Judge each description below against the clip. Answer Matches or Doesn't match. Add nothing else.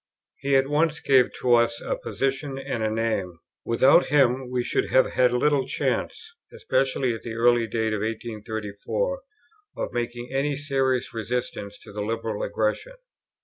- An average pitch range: Matches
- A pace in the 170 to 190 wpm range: Doesn't match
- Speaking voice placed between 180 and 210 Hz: Doesn't match